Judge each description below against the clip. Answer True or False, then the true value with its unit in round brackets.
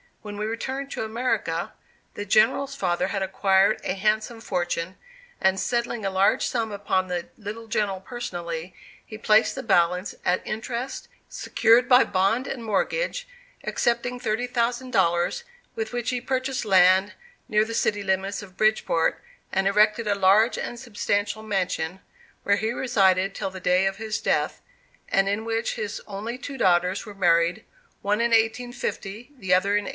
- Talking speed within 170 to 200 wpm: False (160 wpm)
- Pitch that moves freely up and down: False (3.6 semitones)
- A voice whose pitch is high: True (210 Hz)